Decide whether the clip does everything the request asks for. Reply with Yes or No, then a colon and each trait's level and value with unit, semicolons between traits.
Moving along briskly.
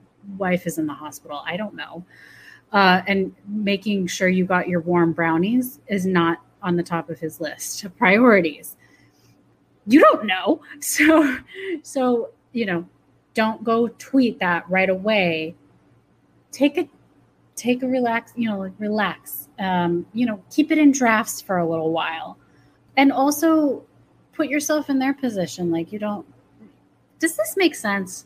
No: average, 155 wpm